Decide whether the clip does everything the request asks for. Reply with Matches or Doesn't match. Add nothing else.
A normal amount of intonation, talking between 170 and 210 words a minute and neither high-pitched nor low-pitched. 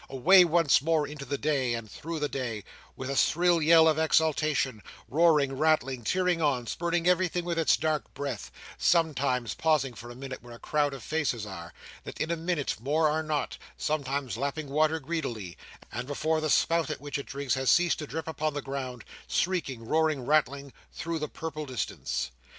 Matches